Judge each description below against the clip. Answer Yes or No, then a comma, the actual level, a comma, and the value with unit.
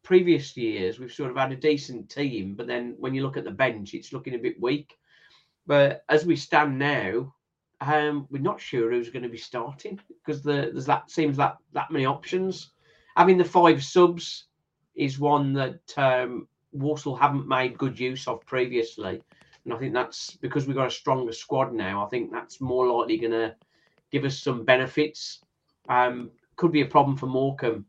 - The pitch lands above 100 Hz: Yes, medium, 140 Hz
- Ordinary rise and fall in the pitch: Yes, average, 3.2 semitones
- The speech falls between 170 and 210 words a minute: Yes, average, 195 wpm